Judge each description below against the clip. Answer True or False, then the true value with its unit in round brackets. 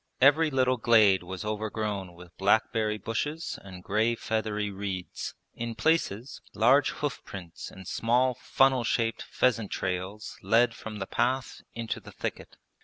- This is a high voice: False (110 Hz)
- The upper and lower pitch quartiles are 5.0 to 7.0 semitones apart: False (4.1 semitones)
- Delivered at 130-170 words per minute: True (140 wpm)